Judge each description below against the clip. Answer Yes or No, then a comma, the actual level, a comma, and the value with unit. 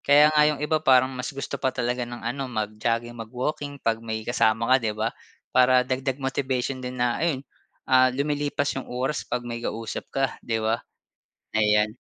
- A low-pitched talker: Yes, low, 125 Hz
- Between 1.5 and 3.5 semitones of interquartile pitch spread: Yes, average, 2.8 semitones